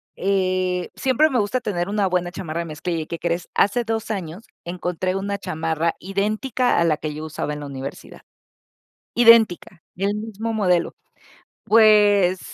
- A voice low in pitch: No, medium, 185 Hz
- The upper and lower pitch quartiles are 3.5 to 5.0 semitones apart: Yes, average, 4.0 semitones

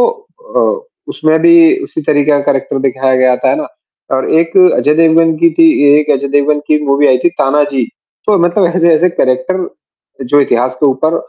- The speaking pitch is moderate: Yes, medium, 150 Hz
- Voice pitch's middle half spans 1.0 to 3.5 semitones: No, average, 4.2 semitones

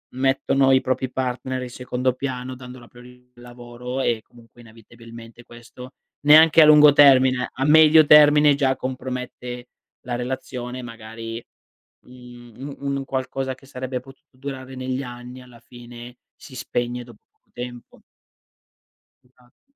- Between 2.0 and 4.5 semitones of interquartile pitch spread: No, narrow, 1.5 semitones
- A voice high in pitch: No, low, 125 Hz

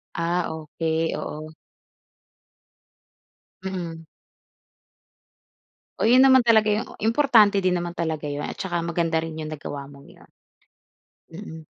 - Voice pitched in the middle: Yes, medium, 170 Hz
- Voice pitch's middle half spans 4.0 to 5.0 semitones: Yes, average, 4.5 semitones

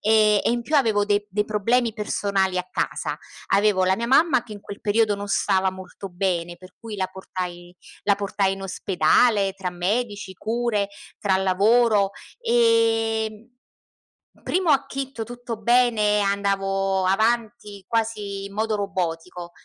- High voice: Yes, high, 205 Hz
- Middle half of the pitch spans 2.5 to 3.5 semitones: Yes, average, 2.9 semitones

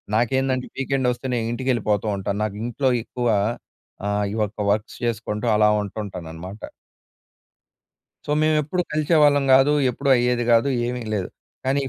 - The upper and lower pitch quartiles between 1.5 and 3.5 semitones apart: No, average, 4.2 semitones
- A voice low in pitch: Yes, low, 120 Hz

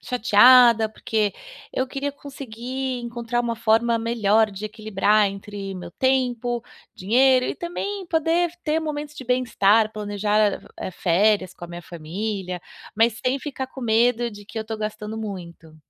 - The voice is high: Yes, high, 225 Hz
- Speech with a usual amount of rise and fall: Yes, average, 3.7 semitones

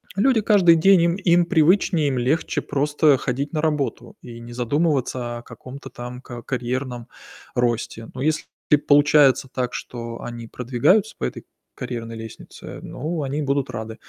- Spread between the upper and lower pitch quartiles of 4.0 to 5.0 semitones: Yes, average, 4.5 semitones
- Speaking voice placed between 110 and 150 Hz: Yes, low, 135 Hz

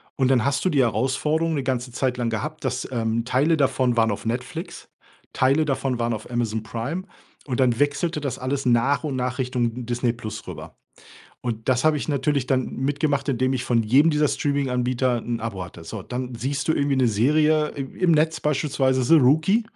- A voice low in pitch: Yes, low, 130 Hz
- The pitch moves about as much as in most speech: Yes, average, 3.2 semitones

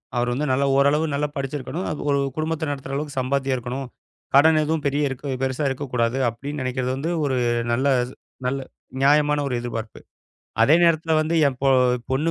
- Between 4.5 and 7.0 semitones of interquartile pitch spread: No, narrow, 2.5 semitones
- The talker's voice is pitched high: No, medium, 140 Hz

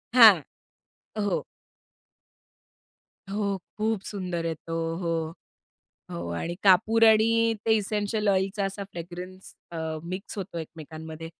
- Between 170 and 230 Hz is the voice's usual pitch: Yes, high, 190 Hz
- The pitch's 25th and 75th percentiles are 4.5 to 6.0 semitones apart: No, average, 3.7 semitones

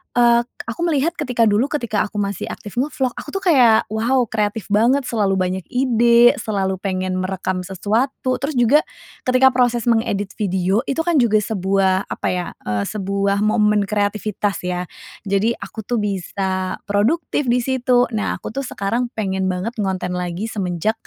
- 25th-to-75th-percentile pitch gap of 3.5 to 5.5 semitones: Yes, average, 4.1 semitones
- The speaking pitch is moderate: No, high, 215 Hz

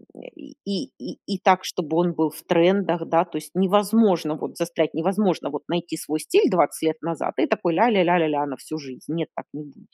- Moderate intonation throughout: Yes, average, 3.3 semitones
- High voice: No, medium, 170 Hz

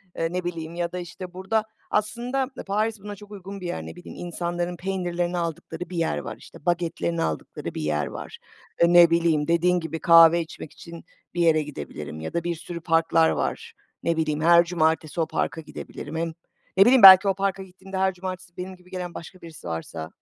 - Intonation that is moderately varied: No, narrow, 2.3 semitones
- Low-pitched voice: No, medium, 175 Hz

